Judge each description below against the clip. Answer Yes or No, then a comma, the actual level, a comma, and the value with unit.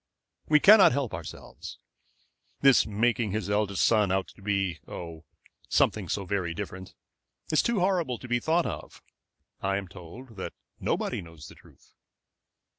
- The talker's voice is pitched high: No, low, 105 Hz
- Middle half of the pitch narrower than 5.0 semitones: No, average, 5.3 semitones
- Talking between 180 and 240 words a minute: No, average, 150 wpm